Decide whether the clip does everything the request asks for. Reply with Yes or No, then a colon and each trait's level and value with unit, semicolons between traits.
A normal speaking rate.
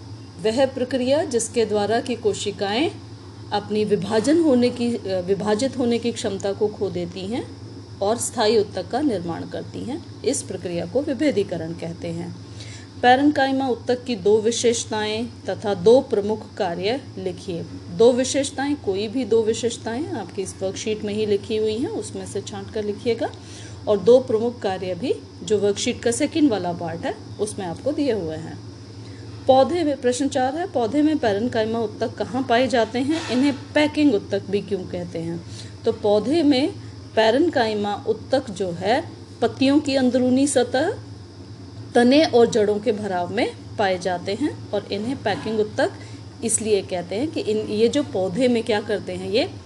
Yes: average, 165 wpm